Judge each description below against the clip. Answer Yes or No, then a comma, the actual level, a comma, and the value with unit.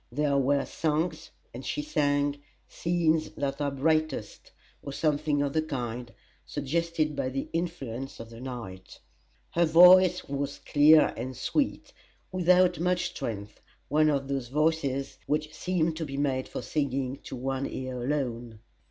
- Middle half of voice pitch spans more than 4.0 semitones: No, average, 3.4 semitones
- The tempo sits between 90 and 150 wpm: Yes, average, 145 wpm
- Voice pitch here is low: No, medium, 145 Hz